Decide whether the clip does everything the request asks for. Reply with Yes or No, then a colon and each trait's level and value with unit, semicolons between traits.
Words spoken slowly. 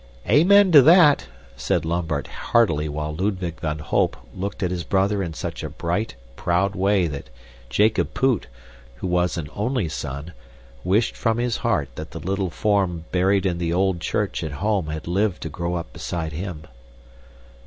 No: average, 170 wpm